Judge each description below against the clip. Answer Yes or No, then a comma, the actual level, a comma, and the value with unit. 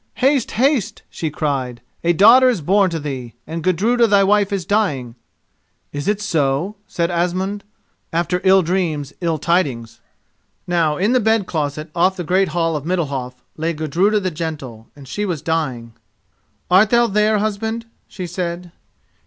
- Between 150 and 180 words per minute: Yes, average, 160 wpm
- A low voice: No, medium, 175 Hz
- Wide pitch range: No, average, 5.0 semitones